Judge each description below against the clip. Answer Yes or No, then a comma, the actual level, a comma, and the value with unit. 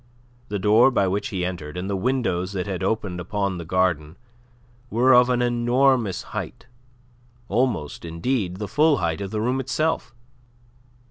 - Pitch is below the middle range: Yes, low, 105 Hz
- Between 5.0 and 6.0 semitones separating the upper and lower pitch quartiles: Yes, average, 5.3 semitones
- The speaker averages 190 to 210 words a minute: No, average, 150 wpm